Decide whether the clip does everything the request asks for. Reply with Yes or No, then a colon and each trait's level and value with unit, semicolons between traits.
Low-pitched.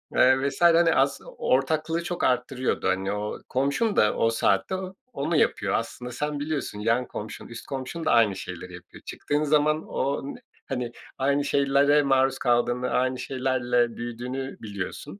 Yes: low, 130 Hz